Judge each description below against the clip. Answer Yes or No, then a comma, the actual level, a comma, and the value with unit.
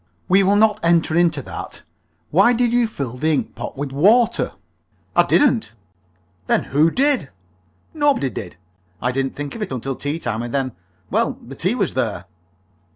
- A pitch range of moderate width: No, wide, 8.4 semitones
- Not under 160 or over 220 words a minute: Yes, average, 170 wpm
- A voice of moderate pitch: Yes, medium, 160 Hz